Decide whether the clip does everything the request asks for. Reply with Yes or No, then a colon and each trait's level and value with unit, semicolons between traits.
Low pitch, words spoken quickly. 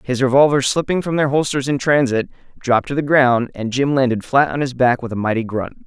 Yes: low, 130 Hz; fast, 235 wpm